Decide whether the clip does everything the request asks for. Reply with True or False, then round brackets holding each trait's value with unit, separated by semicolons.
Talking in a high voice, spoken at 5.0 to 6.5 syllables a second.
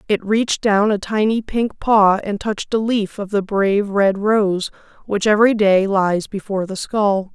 False (205 Hz; 4.6 syllables/s)